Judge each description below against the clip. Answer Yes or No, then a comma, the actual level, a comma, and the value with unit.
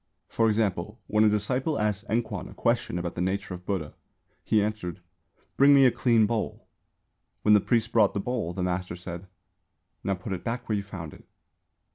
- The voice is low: Yes, low, 105 Hz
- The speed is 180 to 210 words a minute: Yes, average, 190 wpm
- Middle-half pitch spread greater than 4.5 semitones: No, average, 4.0 semitones